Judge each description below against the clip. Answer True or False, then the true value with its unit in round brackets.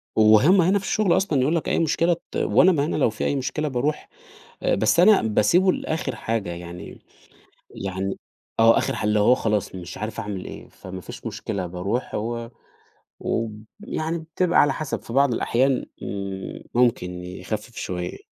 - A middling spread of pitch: False (7.8 semitones)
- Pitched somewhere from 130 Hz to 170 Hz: False (115 Hz)